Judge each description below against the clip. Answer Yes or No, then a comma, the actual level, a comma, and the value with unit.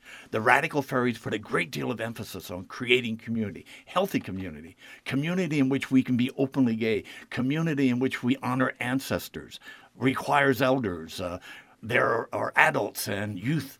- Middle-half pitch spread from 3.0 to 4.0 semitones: Yes, average, 3.5 semitones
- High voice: No, low, 125 Hz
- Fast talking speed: No, average, 155 wpm